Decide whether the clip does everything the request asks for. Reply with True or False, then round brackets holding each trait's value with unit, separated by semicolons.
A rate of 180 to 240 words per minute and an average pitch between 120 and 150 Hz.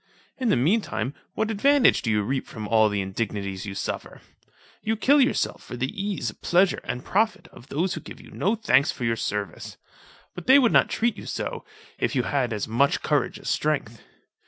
True (205 wpm; 140 Hz)